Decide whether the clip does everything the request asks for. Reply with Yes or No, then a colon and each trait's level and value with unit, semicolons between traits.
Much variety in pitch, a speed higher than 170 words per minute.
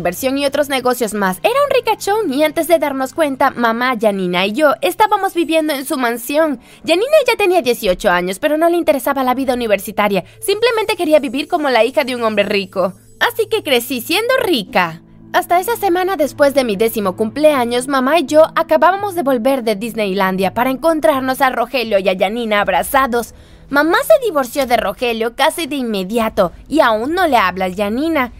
Yes: wide, 6.2 semitones; average, 185 wpm